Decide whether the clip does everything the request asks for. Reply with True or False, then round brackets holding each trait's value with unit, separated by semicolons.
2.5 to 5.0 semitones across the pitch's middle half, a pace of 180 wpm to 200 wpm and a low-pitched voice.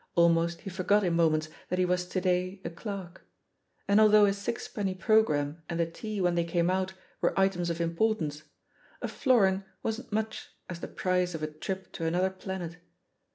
False (2.8 semitones; 190 wpm; 180 Hz)